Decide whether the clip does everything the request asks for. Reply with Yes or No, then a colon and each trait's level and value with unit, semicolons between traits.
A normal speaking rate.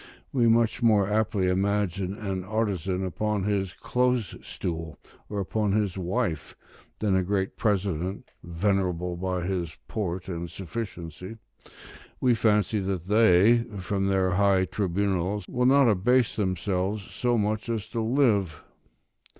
No: slow, 130 wpm